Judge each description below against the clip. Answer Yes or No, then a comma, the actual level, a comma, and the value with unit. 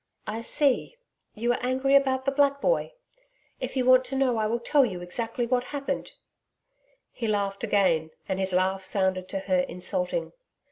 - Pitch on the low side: No, high, 235 Hz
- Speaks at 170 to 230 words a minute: Yes, average, 175 wpm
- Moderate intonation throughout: No, wide, 5.8 semitones